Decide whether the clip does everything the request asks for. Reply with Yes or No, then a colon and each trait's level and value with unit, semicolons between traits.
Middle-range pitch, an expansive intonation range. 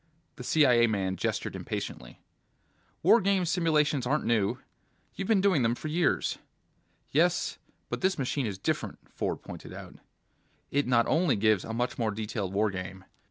No: low, 125 Hz; wide, 7.0 semitones